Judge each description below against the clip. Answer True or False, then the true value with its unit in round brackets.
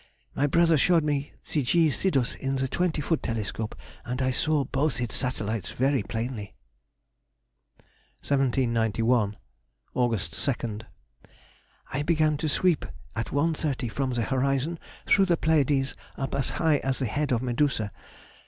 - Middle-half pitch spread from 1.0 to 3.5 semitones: False (4.0 semitones)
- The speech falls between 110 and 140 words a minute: True (135 wpm)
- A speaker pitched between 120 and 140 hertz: True (135 Hz)